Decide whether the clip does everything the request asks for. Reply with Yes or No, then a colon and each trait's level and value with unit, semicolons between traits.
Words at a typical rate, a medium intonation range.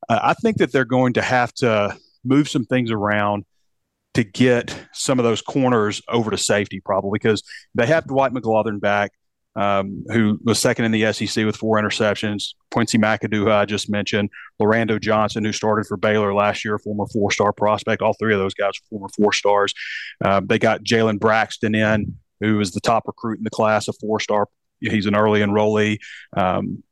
No: average, 185 wpm; narrow, 1.4 semitones